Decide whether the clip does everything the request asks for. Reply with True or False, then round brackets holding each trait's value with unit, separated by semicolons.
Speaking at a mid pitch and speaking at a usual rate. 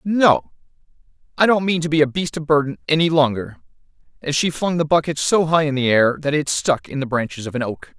False (155 Hz; 235 wpm)